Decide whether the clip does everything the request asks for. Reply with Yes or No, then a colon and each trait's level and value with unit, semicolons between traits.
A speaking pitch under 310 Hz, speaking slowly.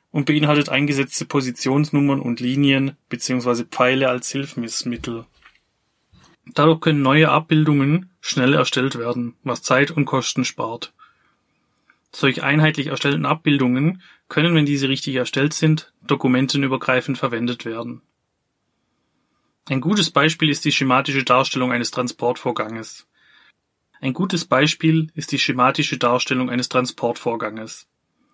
Yes: low, 135 Hz; slow, 110 wpm